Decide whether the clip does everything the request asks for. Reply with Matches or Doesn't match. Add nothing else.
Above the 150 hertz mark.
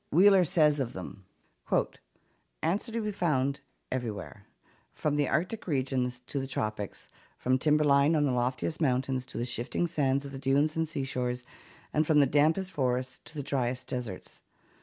Doesn't match